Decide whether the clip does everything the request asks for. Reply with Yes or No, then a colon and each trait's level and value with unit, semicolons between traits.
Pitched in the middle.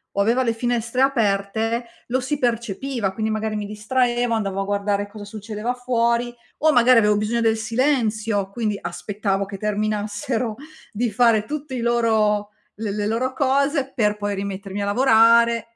No: high, 225 Hz